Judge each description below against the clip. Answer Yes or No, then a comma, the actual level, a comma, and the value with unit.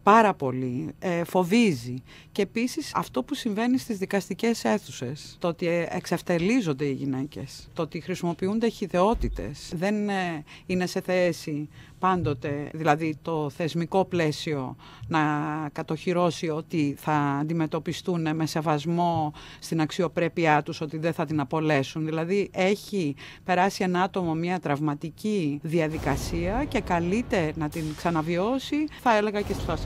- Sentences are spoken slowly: No, average, 125 wpm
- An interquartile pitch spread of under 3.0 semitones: No, average, 3.8 semitones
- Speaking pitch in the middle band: Yes, medium, 165 Hz